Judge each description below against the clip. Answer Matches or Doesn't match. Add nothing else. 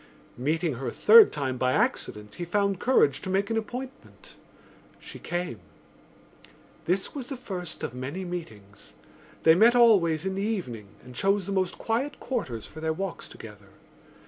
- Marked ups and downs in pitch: Matches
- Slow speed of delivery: Doesn't match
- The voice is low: Doesn't match